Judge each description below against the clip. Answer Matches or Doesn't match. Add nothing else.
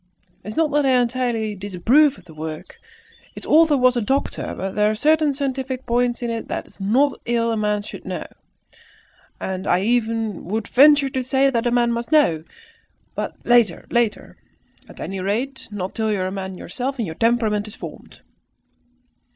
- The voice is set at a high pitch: Matches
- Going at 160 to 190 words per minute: Matches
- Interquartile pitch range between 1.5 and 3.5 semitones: Doesn't match